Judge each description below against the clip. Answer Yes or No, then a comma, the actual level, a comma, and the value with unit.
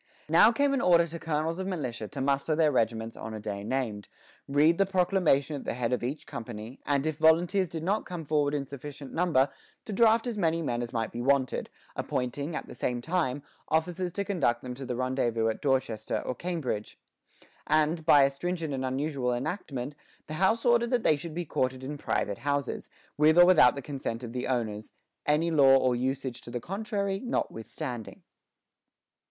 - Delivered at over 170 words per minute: Yes, average, 190 wpm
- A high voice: No, medium, 145 Hz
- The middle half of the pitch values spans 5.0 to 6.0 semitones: Yes, average, 5.3 semitones